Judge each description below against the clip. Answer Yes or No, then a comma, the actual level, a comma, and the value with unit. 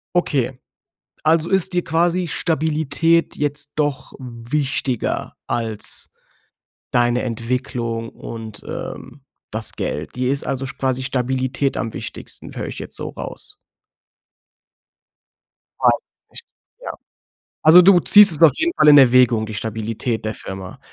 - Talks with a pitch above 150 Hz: No, low, 130 Hz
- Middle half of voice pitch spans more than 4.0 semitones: Yes, average, 5.0 semitones